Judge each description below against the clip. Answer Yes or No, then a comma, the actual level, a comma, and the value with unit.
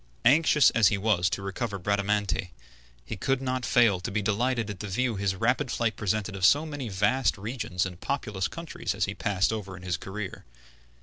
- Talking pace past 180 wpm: Yes, average, 195 wpm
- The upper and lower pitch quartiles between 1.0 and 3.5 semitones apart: No, average, 4.3 semitones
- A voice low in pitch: Yes, low, 105 Hz